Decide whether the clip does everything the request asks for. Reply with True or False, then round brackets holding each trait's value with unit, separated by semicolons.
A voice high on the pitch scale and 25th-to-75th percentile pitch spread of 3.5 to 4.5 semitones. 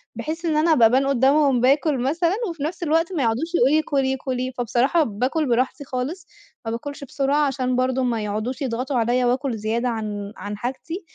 True (265 Hz; 3.8 semitones)